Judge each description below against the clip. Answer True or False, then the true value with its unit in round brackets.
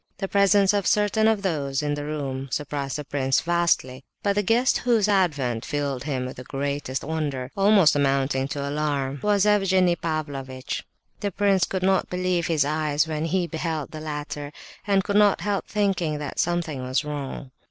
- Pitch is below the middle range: False (155 Hz)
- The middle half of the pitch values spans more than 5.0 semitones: True (5.5 semitones)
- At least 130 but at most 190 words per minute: True (170 wpm)